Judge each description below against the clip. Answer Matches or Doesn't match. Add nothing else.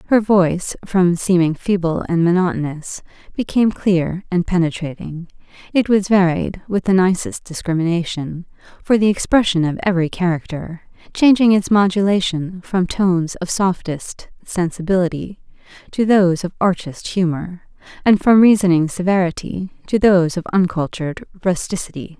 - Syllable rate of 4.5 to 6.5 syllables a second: Matches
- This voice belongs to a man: Doesn't match